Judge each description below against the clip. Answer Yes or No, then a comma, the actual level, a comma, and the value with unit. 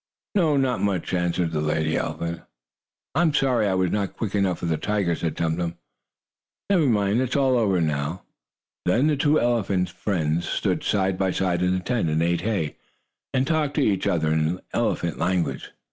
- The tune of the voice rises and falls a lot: Yes, wide, 5.9 semitones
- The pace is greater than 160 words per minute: Yes, average, 190 wpm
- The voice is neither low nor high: No, very low, 95 Hz